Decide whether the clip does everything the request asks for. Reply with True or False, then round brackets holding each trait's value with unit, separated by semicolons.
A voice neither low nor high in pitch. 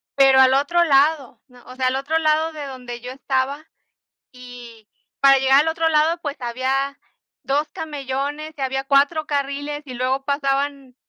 False (275 Hz)